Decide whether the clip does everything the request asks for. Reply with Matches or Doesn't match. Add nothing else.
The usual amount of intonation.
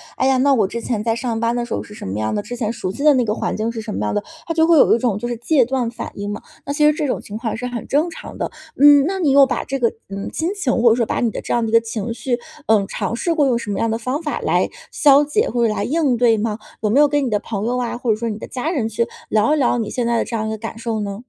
Matches